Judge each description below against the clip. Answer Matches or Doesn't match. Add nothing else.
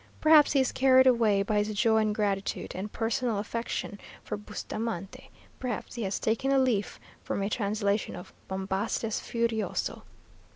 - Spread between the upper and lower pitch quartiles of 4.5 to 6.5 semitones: Doesn't match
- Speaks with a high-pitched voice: Matches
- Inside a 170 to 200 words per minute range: Doesn't match